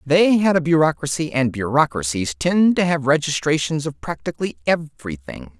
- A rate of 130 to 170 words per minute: Yes, average, 140 wpm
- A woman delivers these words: No, male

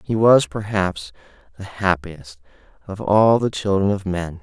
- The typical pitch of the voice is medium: No, very low, 95 Hz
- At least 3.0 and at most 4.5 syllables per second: Yes, 4.1 syllables/s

